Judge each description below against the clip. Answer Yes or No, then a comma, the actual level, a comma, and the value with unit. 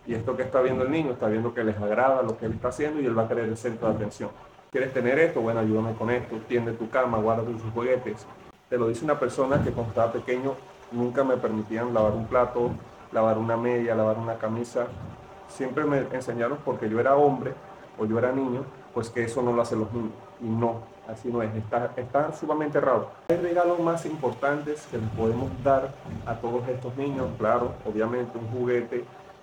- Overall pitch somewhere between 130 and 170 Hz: No, low, 120 Hz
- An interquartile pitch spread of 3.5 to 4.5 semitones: No, narrow, 2.5 semitones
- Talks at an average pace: No, fast, 210 wpm